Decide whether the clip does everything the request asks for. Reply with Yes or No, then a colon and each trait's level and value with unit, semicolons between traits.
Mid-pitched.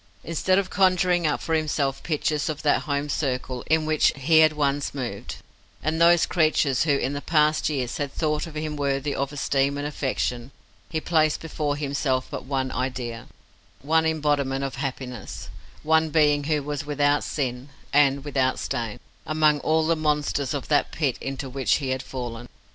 Yes: medium, 145 Hz